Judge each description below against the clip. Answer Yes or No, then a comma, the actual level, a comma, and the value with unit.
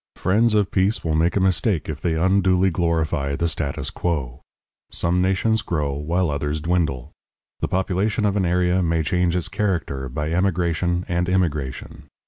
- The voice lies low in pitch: Yes, very low, 85 Hz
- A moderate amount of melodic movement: Yes, average, 3.1 semitones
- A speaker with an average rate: Yes, average, 160 wpm